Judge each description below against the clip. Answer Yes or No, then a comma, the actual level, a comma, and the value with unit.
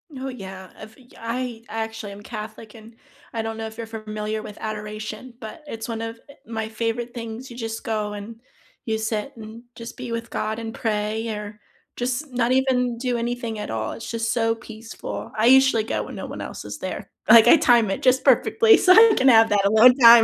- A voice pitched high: Yes, high, 225 Hz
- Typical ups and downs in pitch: No, narrow, 2.0 semitones